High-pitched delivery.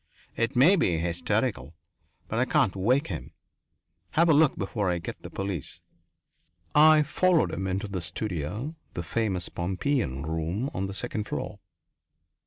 No: low, 100 Hz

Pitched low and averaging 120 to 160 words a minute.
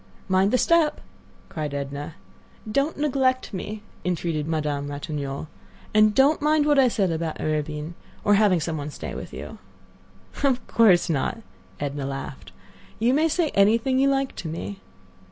No: high, 195 Hz; average, 155 wpm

